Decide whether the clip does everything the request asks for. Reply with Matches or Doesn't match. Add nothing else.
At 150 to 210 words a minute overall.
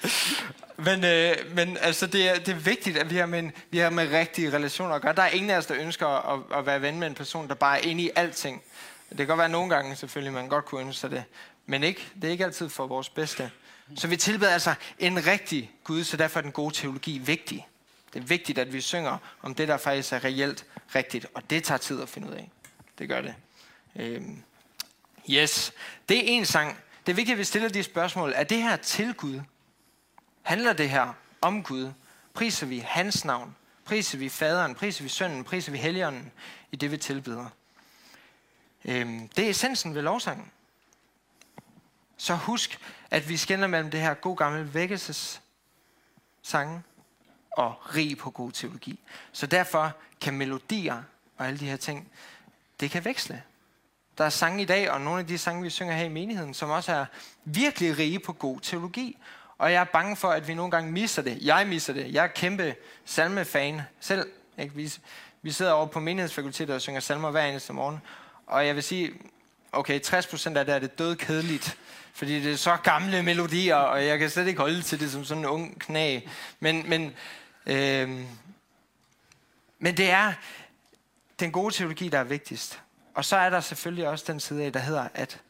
Matches